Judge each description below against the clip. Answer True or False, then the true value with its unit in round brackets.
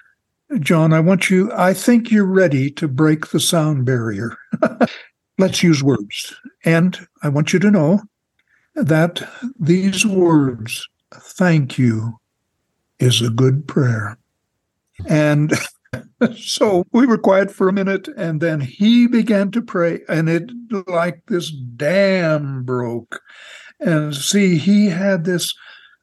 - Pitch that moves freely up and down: True (6.0 semitones)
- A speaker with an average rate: False (130 wpm)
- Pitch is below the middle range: False (170 Hz)